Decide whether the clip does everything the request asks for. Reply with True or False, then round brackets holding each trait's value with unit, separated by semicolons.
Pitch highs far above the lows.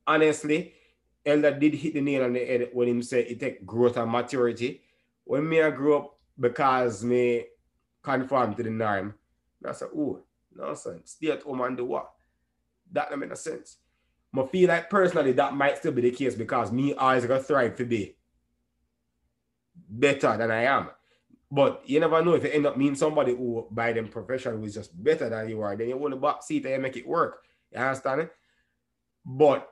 False (4.1 semitones)